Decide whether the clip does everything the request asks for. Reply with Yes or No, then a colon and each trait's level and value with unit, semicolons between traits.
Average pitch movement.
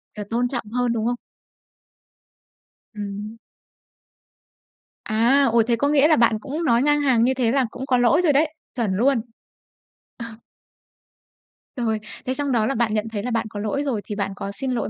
Yes: average, 3.7 semitones